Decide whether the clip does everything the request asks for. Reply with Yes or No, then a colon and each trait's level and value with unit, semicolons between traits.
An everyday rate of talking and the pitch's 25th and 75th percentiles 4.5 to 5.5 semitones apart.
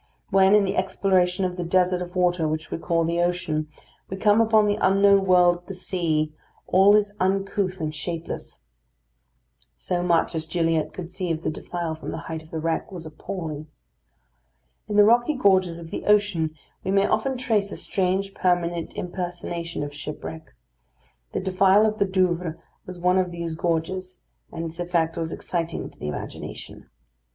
No: average, 175 wpm; average, 2.7 semitones